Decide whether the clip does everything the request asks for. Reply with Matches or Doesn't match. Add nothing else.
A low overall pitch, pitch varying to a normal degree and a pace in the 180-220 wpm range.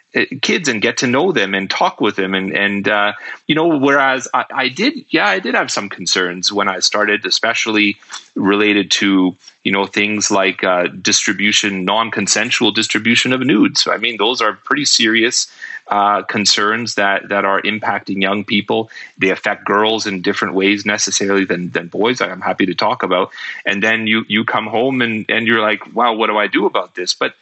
Doesn't match